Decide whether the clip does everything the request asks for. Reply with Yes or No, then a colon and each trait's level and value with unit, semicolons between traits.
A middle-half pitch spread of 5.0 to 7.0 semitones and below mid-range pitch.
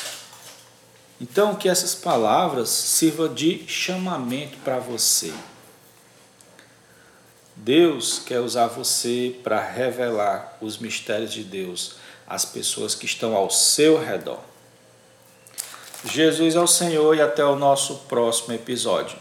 Yes: wide, 5.4 semitones; low, 130 Hz